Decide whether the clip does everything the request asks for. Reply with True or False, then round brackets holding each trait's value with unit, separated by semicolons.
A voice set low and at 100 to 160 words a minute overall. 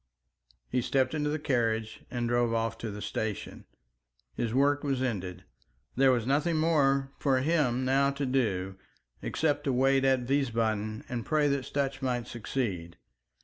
True (130 Hz; 155 wpm)